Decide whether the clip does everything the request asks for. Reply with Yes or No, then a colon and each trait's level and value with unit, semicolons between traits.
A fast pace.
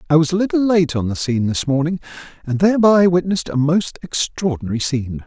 No: average, 195 wpm